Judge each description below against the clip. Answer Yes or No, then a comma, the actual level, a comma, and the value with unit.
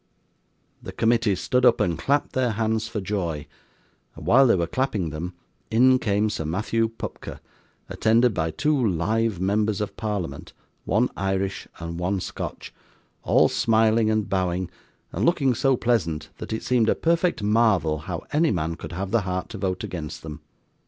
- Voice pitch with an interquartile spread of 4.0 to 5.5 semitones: Yes, average, 4.5 semitones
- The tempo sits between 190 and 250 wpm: No, average, 165 wpm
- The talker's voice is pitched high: No, low, 105 Hz